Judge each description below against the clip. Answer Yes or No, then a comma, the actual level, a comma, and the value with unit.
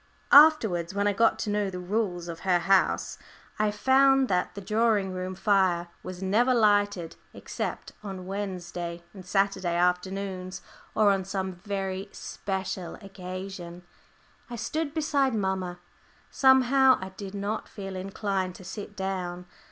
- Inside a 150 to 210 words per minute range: No, average, 140 wpm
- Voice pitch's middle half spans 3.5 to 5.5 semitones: No, narrow, 2.4 semitones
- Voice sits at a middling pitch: No, high, 195 Hz